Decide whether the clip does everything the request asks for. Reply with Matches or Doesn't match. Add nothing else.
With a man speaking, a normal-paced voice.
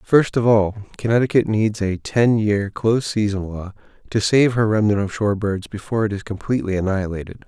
Matches